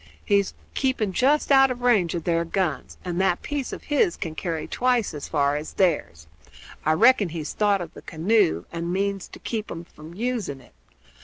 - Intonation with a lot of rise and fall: Yes, wide, 6.4 semitones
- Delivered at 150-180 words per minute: No, average, 190 wpm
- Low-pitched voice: No, medium, 185 Hz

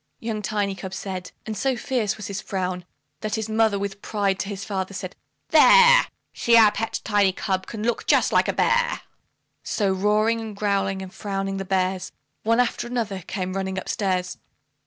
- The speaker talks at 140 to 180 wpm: No, average, 190 wpm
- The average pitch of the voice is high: Yes, high, 200 Hz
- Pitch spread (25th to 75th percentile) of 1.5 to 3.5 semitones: Yes, narrow, 2.5 semitones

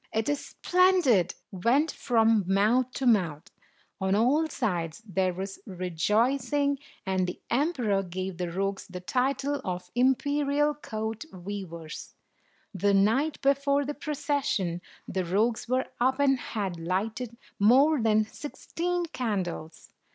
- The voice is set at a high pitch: Yes, high, 225 Hz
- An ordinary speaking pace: No, slow, 125 wpm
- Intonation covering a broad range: Yes, wide, 6.7 semitones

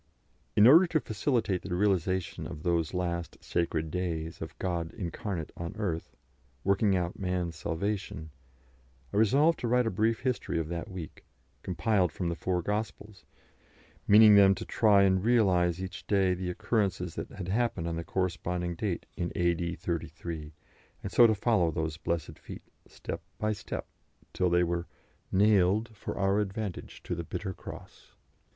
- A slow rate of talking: No, average, 160 wpm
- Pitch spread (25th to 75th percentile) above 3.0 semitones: Yes, average, 3.5 semitones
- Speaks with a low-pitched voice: Yes, very low, 95 Hz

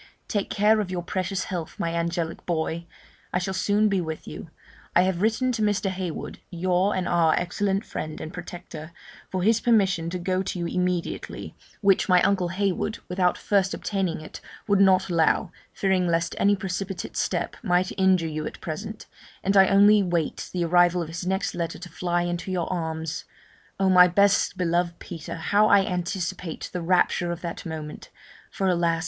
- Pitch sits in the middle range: Yes, medium, 180 Hz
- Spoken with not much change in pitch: Yes, narrow, 2.3 semitones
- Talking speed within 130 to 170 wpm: No, average, 180 wpm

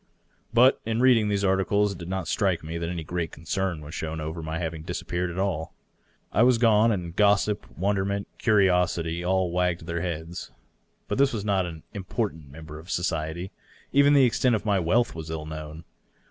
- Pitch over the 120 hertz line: No, very low, 90 Hz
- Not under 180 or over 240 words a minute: Yes, average, 190 wpm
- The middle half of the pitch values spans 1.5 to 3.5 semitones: No, average, 3.9 semitones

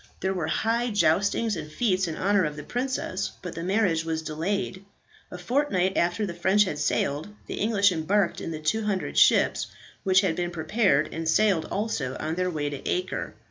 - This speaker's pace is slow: No, average, 185 wpm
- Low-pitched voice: No, medium, 185 Hz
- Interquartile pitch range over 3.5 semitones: Yes, average, 4.2 semitones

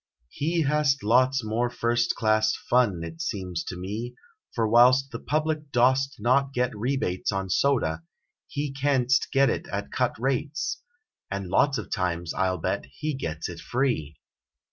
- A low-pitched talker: Yes, low, 125 Hz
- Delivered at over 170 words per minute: No, average, 165 wpm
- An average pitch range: No, wide, 5.7 semitones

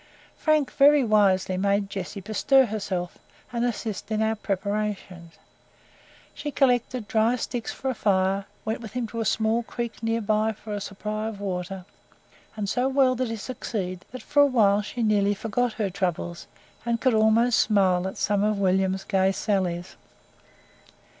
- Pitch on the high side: Yes, high, 215 Hz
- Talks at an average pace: Yes, average, 160 wpm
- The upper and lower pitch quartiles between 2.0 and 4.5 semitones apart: Yes, average, 3.4 semitones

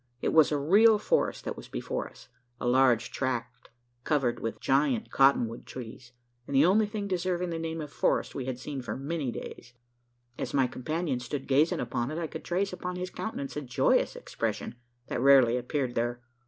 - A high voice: No, medium, 140 Hz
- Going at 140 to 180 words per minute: No, average, 195 wpm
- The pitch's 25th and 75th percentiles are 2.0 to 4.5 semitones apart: No, wide, 5.5 semitones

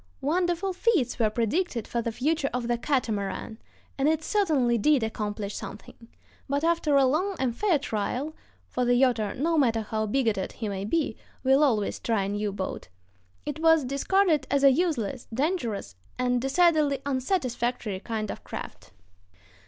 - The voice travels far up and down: Yes, wide, 5.8 semitones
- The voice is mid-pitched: No, very high, 260 Hz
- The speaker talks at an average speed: Yes, average, 160 wpm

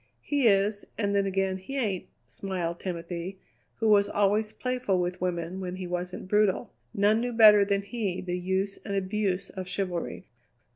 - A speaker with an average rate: Yes, average, 165 wpm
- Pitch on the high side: Yes, high, 195 Hz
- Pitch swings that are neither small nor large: No, narrow, 2.3 semitones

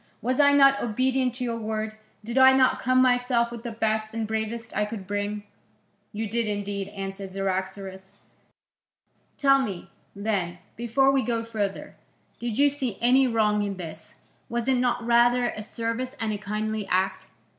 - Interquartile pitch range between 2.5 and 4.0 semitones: Yes, average, 3.3 semitones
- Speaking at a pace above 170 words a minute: No, average, 165 wpm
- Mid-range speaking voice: No, high, 225 Hz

